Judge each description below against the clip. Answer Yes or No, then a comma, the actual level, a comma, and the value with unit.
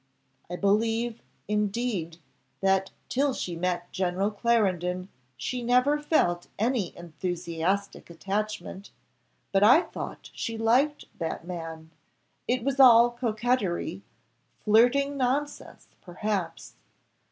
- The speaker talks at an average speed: No, slow, 100 wpm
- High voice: Yes, high, 210 Hz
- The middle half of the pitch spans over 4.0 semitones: Yes, average, 5.2 semitones